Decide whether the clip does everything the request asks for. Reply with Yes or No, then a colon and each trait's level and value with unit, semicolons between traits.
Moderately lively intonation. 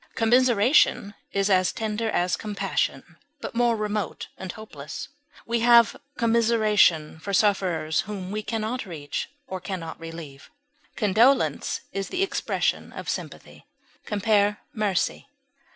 Yes: average, 3.6 semitones